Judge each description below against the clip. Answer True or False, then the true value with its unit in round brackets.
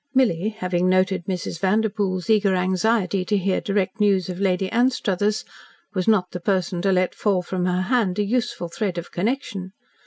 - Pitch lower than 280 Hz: True (190 Hz)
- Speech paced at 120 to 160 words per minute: False (175 wpm)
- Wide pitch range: False (2.5 semitones)